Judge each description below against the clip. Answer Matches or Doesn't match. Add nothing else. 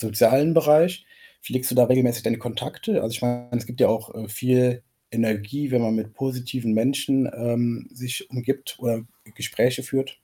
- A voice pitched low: Matches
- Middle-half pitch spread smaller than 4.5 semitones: Matches